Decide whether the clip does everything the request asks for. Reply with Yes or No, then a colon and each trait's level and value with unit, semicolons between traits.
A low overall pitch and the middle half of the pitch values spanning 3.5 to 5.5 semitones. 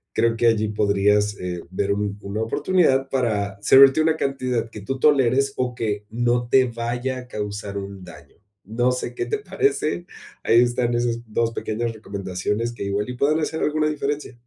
Yes: low, 120 Hz; average, 4.2 semitones